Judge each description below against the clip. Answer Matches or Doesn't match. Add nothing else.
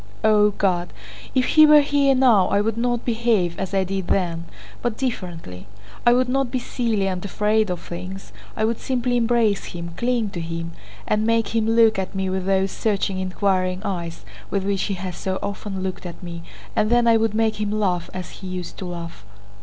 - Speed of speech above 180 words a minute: Matches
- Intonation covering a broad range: Doesn't match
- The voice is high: Matches